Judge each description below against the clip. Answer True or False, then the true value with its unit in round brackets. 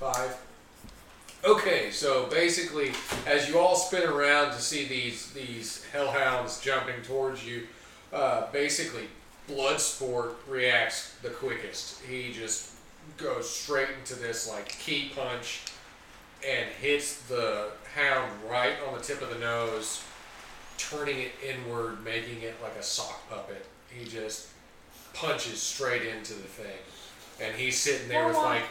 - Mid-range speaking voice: False (125 Hz)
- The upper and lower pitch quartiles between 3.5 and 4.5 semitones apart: True (3.9 semitones)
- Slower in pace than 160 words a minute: True (135 wpm)